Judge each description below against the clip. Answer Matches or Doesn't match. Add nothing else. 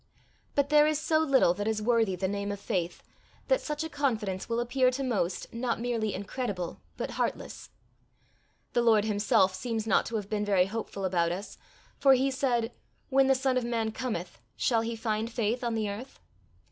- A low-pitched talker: Doesn't match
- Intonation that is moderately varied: Matches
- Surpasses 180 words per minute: Matches